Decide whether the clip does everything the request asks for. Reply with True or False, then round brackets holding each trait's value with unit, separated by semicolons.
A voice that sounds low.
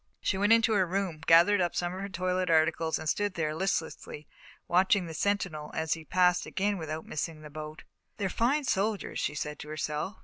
False (175 Hz)